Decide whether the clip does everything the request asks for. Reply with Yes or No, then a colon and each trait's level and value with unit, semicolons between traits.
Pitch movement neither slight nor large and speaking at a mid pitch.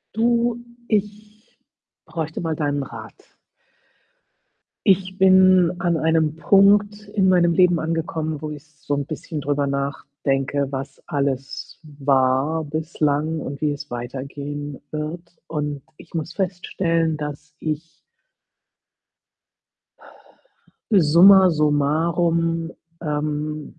Yes: average, 3.3 semitones; medium, 155 Hz